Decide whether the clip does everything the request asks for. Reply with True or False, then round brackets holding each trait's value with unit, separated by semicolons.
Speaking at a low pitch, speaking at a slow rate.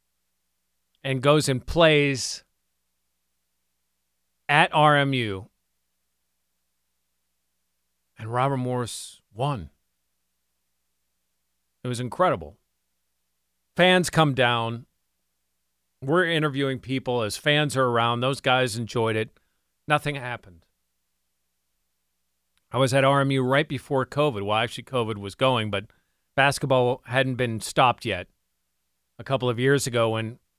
True (105 Hz; 105 wpm)